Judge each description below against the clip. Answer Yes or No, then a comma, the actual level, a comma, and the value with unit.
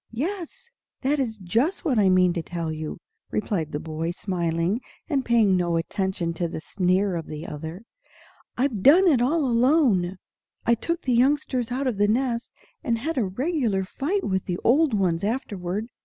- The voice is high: Yes, high, 215 Hz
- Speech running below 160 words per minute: No, average, 175 wpm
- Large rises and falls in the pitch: Yes, wide, 7.0 semitones